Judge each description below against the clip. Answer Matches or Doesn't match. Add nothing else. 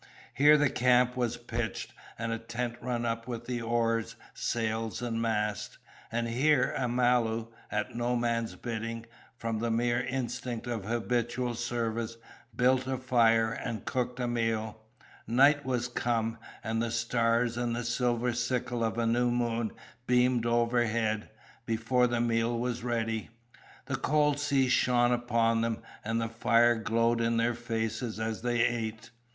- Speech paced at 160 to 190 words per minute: Doesn't match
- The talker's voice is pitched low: Matches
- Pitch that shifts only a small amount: Matches